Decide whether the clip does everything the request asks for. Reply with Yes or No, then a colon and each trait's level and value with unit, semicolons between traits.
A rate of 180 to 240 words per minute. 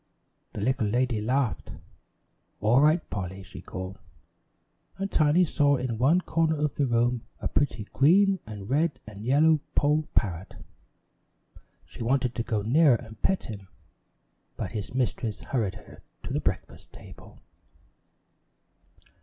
No: slow, 135 wpm